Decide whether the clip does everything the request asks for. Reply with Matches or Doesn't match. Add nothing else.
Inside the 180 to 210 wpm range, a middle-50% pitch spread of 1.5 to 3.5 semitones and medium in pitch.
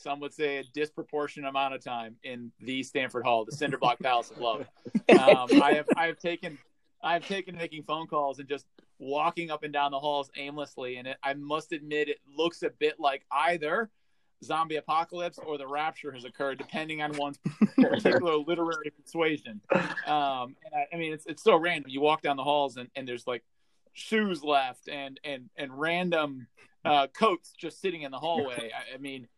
Matches